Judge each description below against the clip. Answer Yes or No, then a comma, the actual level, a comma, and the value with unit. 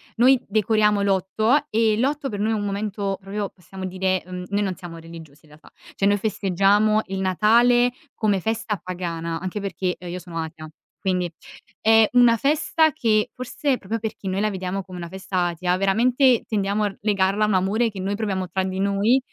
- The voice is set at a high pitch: Yes, high, 200 Hz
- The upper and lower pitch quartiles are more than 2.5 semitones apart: Yes, average, 2.9 semitones